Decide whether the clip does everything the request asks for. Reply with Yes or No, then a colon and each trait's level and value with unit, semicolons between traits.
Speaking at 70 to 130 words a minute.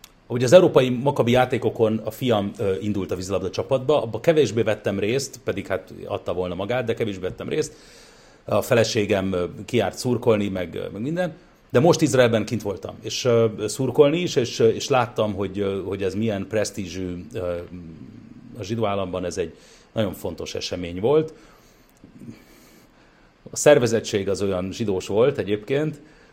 No: average, 150 wpm